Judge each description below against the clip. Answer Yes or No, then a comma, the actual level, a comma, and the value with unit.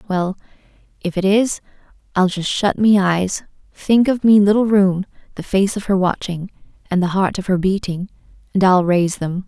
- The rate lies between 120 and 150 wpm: No, average, 185 wpm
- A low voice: No, high, 190 Hz